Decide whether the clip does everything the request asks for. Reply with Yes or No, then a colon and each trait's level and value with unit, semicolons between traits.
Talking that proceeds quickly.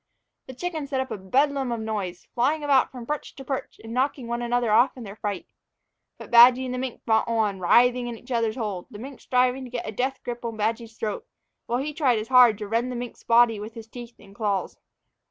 Yes: fast, 235 wpm